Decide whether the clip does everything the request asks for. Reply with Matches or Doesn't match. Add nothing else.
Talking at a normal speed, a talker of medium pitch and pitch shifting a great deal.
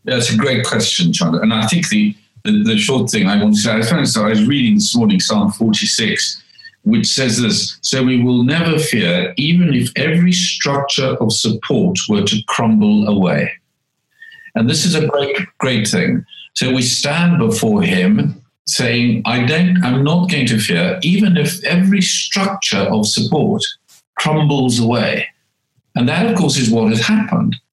Matches